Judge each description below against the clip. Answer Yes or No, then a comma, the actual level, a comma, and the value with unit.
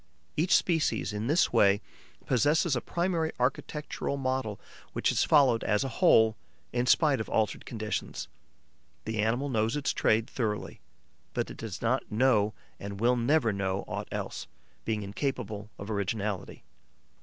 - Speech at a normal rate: Yes, average, 145 wpm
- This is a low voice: Yes, low, 115 Hz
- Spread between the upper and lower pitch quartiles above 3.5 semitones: Yes, average, 4.5 semitones